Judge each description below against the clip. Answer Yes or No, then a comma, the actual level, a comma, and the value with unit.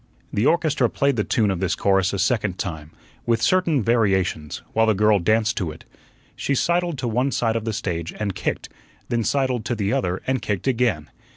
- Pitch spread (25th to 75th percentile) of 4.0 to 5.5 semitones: Yes, average, 4.6 semitones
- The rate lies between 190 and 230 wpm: Yes, average, 200 wpm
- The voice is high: No, low, 110 Hz